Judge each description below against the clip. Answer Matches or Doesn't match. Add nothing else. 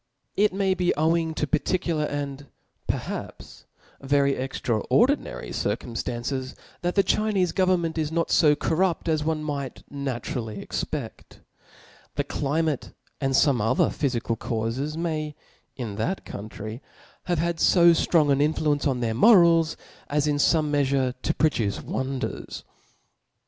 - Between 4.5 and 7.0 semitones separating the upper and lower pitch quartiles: Doesn't match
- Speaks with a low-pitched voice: Doesn't match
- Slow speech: Doesn't match